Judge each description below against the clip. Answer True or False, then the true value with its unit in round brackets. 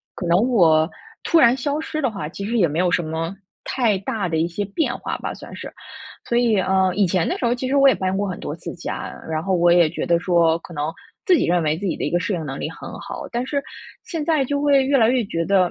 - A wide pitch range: True (6.4 semitones)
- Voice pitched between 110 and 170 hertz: False (195 Hz)